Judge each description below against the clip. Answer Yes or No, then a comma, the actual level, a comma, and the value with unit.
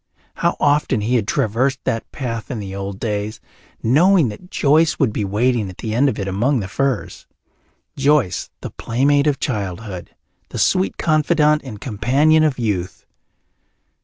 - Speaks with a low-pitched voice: Yes, low, 125 Hz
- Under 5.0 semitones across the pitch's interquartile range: No, wide, 5.5 semitones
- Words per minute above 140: Yes, average, 160 wpm